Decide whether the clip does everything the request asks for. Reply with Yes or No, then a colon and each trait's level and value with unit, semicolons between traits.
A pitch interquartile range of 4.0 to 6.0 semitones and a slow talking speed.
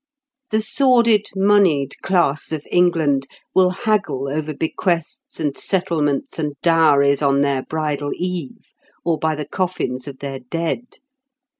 Yes: average, 4.6 semitones; slow, 130 wpm